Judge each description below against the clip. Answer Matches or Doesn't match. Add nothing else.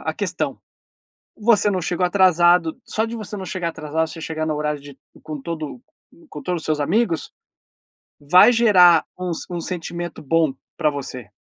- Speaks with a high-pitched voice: Doesn't match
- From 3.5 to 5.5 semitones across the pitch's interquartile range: Doesn't match